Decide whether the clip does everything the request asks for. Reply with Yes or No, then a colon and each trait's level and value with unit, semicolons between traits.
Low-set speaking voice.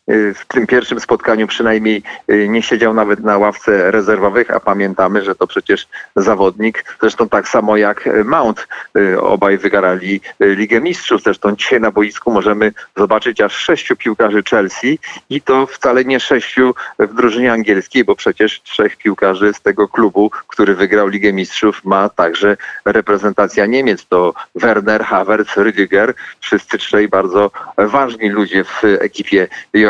Yes: low, 105 Hz